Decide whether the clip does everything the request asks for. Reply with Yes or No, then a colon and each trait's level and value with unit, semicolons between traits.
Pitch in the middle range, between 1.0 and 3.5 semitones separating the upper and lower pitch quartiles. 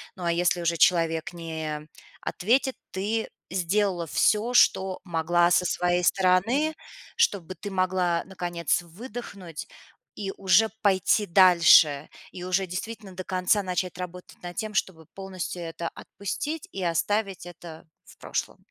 Yes: medium, 180 Hz; narrow, 2.5 semitones